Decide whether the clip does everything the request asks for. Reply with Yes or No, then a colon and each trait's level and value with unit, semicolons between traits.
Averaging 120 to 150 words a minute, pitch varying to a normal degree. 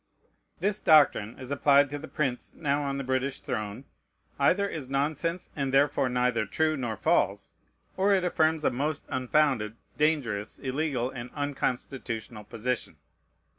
Yes: average, 140 wpm; average, 3.5 semitones